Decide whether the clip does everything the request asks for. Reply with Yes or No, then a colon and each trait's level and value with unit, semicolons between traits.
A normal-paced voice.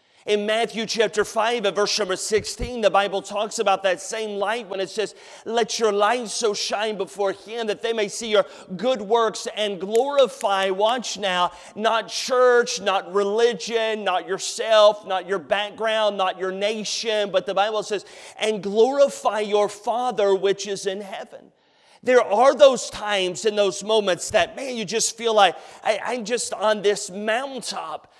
Yes: average, 170 wpm